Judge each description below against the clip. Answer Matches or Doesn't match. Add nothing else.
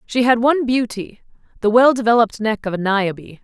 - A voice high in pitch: Matches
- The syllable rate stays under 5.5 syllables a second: Doesn't match